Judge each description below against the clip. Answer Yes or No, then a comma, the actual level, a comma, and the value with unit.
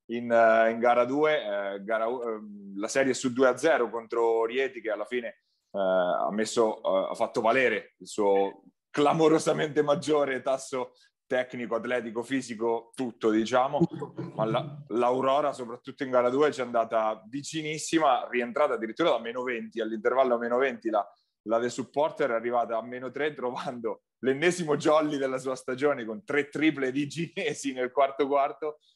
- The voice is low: Yes, low, 125 Hz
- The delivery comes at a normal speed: Yes, average, 155 wpm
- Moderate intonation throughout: Yes, average, 4.0 semitones